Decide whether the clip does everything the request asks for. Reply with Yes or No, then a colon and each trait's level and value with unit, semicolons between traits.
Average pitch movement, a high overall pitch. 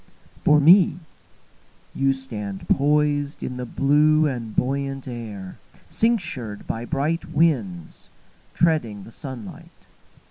No: average, 4.7 semitones; low, 135 Hz